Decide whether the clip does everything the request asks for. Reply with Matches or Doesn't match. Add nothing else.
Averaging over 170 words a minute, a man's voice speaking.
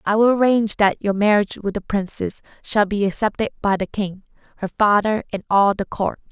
Doesn't match